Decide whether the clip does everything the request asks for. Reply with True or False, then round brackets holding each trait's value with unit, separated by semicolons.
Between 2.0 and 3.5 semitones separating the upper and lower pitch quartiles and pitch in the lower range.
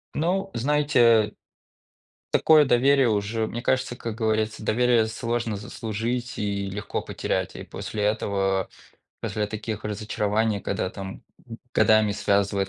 True (2.6 semitones; 110 Hz)